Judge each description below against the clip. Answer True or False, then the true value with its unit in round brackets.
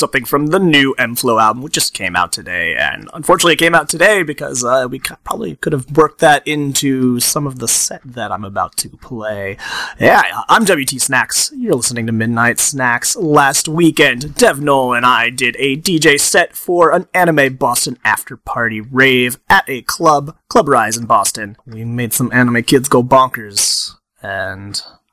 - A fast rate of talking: False (190 wpm)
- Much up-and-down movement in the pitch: False (4.0 semitones)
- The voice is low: True (130 Hz)